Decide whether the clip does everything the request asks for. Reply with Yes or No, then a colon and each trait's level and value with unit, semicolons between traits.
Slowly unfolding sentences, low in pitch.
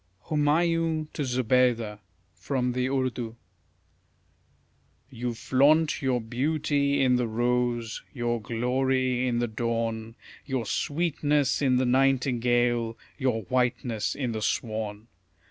Yes: slow, 110 wpm; low, 125 Hz